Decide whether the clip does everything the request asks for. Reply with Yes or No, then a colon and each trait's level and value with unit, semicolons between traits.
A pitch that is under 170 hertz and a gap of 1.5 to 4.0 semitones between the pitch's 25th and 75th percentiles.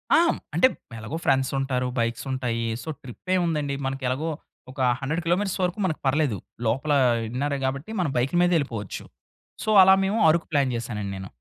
No: medium, 140 Hz; average, 4.8 semitones